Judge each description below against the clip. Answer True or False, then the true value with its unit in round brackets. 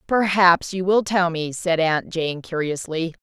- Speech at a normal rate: True (165 wpm)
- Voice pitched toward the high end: False (175 Hz)